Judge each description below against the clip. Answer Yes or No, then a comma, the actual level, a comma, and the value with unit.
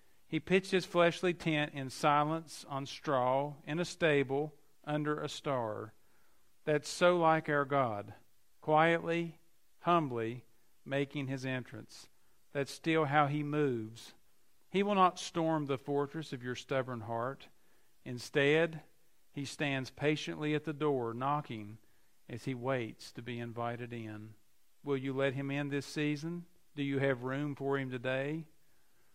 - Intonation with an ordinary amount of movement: Yes, average, 3.3 semitones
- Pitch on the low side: No, medium, 145 Hz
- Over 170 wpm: No, average, 140 wpm